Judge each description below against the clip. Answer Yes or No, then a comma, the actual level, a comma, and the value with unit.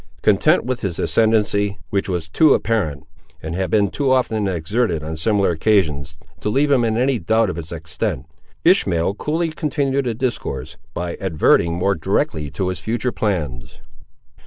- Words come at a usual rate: Yes, average, 160 wpm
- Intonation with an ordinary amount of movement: No, wide, 6.1 semitones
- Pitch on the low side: Yes, low, 100 Hz